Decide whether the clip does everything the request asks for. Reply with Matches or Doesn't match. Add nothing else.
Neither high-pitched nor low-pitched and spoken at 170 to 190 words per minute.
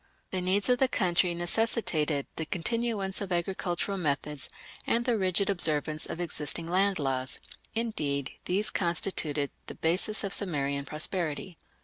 Doesn't match